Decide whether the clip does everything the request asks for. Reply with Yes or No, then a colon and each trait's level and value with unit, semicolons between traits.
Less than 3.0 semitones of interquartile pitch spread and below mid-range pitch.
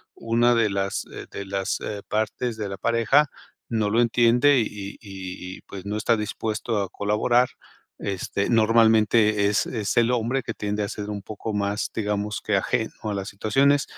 Yes: narrow, 2.4 semitones; low, 105 Hz